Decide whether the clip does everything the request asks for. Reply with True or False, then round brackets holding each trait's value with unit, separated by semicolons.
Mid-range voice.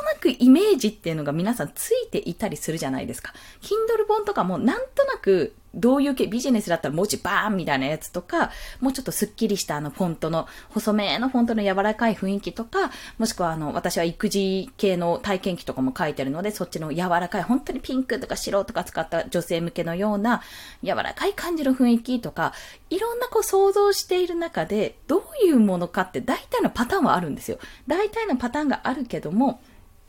False (220 Hz)